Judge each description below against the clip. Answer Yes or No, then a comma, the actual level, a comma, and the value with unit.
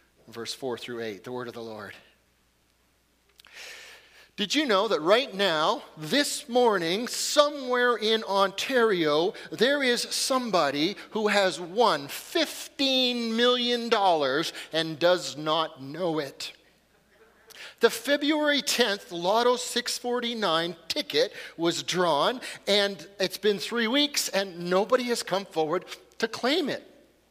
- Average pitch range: No, wide, 7.6 semitones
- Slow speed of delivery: Yes, slow, 120 wpm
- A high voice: Yes, high, 205 Hz